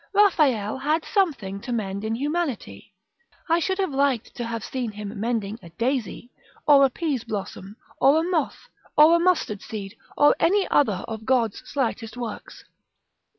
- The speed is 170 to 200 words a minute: No, average, 160 wpm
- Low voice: No, high, 245 Hz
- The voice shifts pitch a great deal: Yes, wide, 5.9 semitones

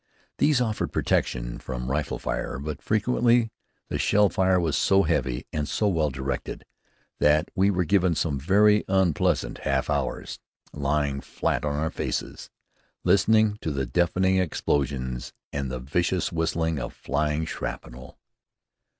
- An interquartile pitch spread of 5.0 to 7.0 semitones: Yes, wide, 5.6 semitones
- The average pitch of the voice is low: Yes, very low, 80 Hz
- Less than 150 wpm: Yes, average, 140 wpm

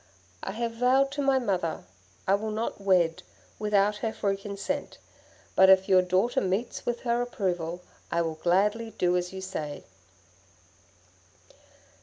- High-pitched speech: Yes, high, 195 Hz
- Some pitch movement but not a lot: Yes, average, 4.1 semitones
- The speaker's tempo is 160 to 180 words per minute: No, average, 145 wpm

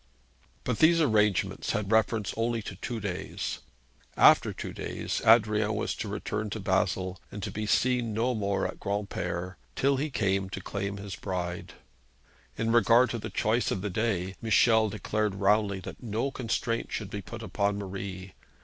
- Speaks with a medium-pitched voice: No, low, 105 Hz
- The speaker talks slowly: No, average, 165 wpm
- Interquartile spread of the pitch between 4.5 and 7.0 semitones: No, narrow, 2.6 semitones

